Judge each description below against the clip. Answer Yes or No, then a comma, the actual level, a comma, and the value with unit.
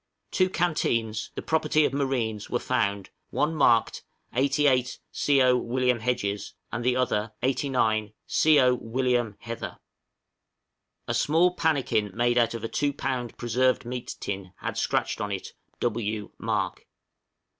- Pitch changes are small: No, average, 3.5 semitones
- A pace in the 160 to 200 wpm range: No, slow, 135 wpm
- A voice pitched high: No, low, 125 Hz